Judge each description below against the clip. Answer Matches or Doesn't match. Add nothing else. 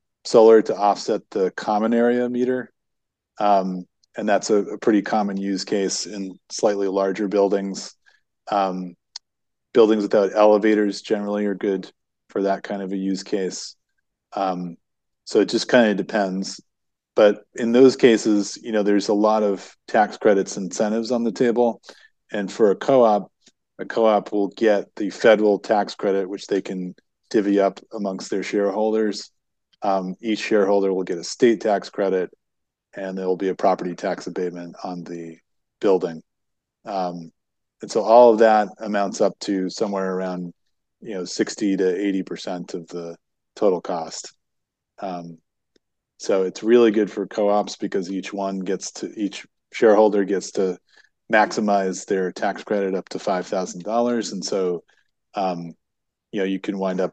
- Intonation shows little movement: Matches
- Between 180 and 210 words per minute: Doesn't match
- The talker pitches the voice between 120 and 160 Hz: Doesn't match